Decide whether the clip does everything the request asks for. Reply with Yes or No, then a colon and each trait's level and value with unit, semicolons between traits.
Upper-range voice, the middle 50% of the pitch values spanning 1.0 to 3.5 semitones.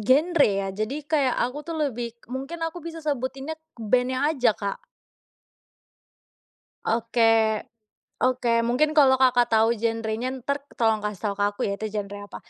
No: high, 245 Hz; average, 4.1 semitones